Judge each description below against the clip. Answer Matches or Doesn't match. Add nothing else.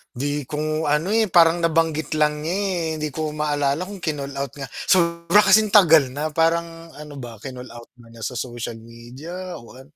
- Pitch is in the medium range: Matches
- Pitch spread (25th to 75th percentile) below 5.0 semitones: Matches